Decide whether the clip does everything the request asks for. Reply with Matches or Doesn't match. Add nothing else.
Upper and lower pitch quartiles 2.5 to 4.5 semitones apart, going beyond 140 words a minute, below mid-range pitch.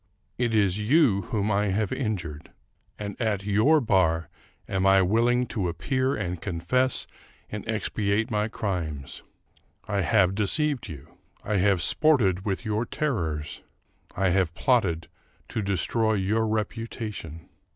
Doesn't match